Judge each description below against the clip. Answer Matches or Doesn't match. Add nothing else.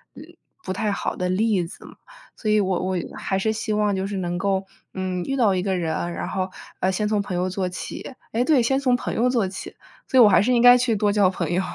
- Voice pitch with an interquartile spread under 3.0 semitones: Doesn't match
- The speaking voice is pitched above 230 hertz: Doesn't match